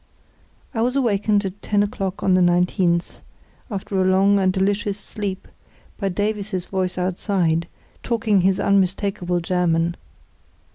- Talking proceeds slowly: Yes, slow, 130 wpm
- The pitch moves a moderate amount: No, narrow, 2.2 semitones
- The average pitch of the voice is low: No, high, 190 Hz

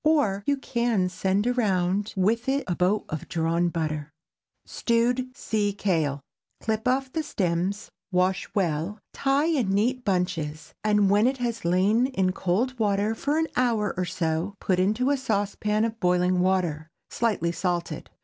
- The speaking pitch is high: Yes, high, 200 Hz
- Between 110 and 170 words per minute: Yes, average, 150 wpm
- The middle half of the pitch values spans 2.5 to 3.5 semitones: No, average, 4.8 semitones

